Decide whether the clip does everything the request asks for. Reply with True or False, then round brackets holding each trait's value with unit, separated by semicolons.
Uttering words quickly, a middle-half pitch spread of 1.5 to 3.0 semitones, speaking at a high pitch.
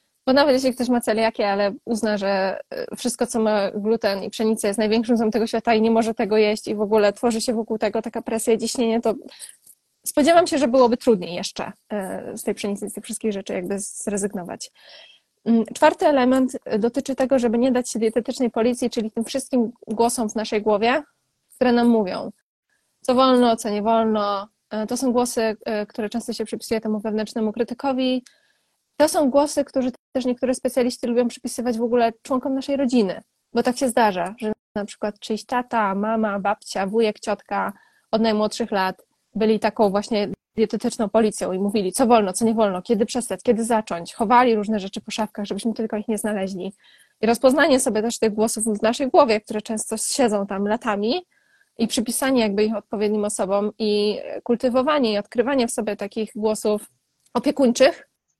True (180 wpm; 2.6 semitones; 225 Hz)